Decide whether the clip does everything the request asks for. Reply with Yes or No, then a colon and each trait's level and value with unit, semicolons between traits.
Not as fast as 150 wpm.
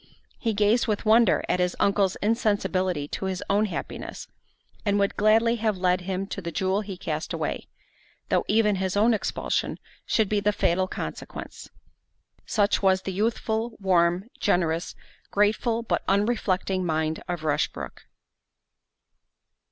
Yes: average, 140 wpm